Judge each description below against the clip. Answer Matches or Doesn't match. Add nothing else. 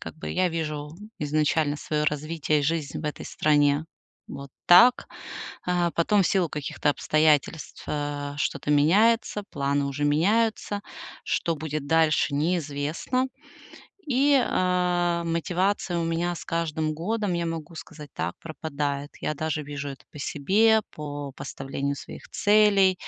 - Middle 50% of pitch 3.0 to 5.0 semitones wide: Matches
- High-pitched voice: Doesn't match